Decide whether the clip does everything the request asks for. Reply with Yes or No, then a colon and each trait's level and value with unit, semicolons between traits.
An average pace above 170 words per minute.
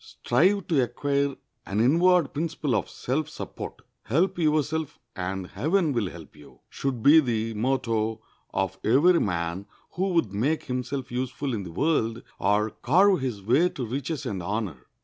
No: average, 155 wpm